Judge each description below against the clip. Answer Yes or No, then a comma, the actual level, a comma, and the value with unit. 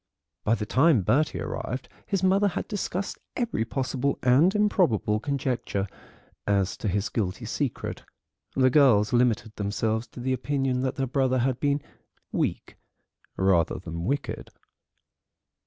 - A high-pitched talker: No, low, 130 Hz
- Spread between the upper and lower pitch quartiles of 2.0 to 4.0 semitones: No, average, 5.0 semitones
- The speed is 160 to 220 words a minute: No, slow, 135 wpm